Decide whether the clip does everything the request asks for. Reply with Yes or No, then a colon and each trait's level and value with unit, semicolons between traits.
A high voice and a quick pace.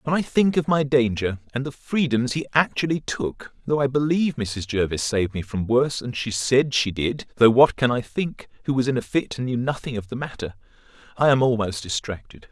No: low, 125 Hz; fast, 220 wpm